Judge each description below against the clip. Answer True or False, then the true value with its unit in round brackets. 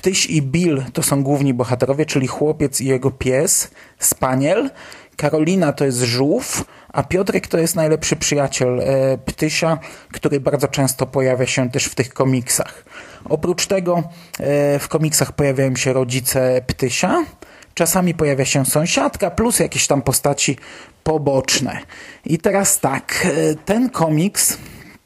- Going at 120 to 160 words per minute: True (140 wpm)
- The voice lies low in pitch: False (145 Hz)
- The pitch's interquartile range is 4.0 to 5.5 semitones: False (3.4 semitones)